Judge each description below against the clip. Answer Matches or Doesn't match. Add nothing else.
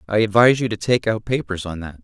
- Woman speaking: Doesn't match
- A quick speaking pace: Matches